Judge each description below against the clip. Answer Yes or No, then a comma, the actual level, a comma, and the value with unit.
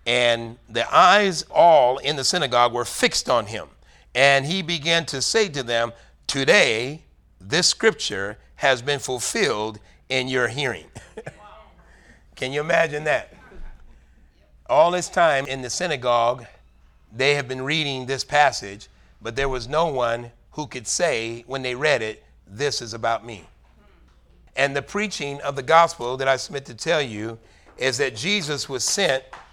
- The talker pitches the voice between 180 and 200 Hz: No, low, 125 Hz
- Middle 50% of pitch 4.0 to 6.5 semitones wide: Yes, average, 4.8 semitones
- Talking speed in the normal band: Yes, average, 155 wpm